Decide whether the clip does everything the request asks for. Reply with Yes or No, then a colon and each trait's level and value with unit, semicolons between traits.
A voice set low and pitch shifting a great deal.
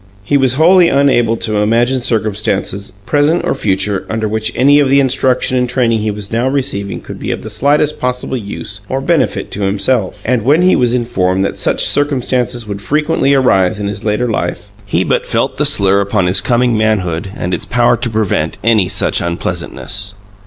No: low, 115 Hz; average, 4.5 semitones